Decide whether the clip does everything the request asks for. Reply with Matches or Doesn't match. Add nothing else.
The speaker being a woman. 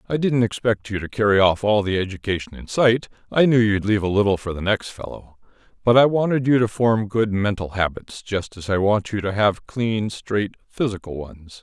Doesn't match